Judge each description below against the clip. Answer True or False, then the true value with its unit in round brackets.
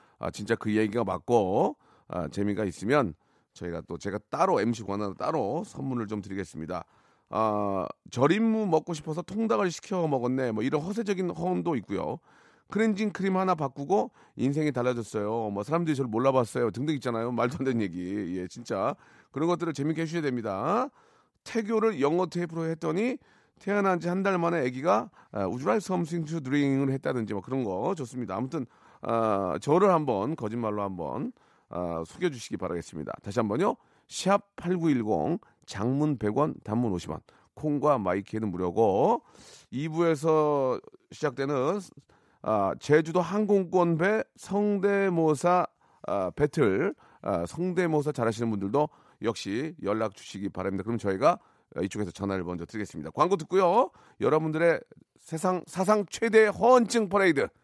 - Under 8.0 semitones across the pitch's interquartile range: False (9.0 semitones)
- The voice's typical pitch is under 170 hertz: True (140 Hz)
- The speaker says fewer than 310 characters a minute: False (325 characters per minute)